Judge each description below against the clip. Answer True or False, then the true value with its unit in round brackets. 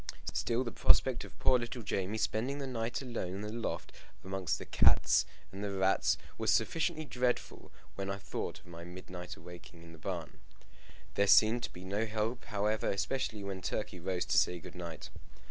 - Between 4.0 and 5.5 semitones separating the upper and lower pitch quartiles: True (4.4 semitones)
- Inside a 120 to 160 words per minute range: False (180 wpm)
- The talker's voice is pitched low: True (100 Hz)